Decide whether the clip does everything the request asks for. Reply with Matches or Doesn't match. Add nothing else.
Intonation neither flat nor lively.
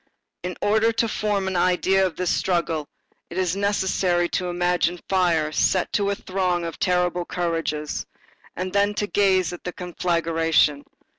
Doesn't match